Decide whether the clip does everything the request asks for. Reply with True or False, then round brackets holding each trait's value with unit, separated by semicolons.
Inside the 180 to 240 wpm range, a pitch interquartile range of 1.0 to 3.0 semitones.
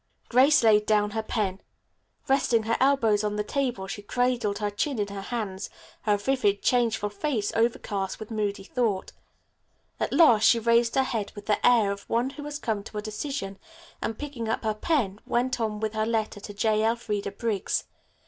True (185 wpm; 2.7 semitones)